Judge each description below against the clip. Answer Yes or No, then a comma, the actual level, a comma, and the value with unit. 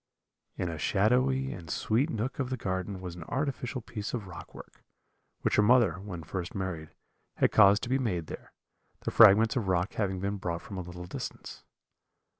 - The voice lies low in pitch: Yes, low, 100 Hz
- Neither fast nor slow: Yes, average, 190 wpm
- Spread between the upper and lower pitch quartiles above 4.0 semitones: Yes, average, 5.0 semitones